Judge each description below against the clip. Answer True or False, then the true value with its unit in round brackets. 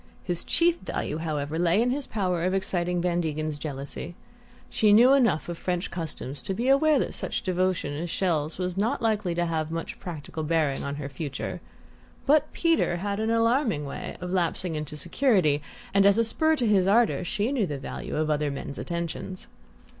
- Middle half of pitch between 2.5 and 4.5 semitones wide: False (5.5 semitones)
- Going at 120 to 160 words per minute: False (190 wpm)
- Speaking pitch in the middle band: True (180 Hz)